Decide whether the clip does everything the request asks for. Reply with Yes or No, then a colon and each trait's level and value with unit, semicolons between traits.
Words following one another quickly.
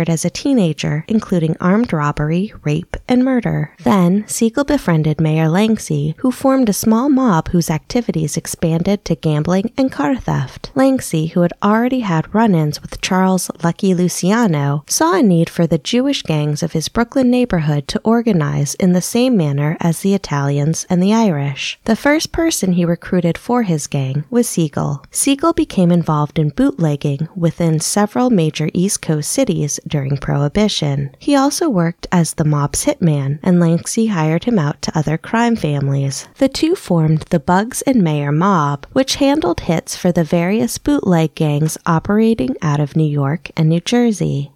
No: average, 165 wpm